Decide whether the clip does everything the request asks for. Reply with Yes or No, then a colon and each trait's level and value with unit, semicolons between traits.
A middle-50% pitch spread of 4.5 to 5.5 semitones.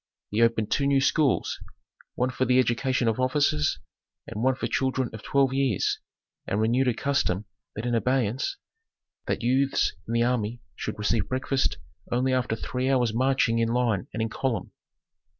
No: narrow, 2.5 semitones